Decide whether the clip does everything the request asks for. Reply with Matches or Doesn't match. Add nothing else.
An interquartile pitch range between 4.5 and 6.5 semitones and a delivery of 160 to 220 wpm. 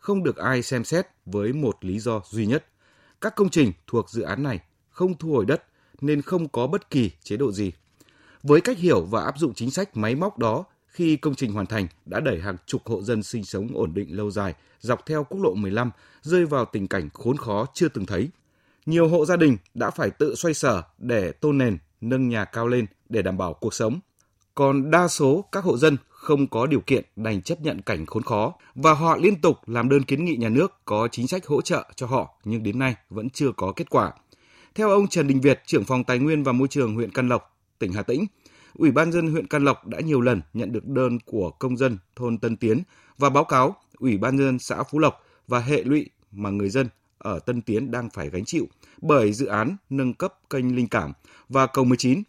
Doesn't match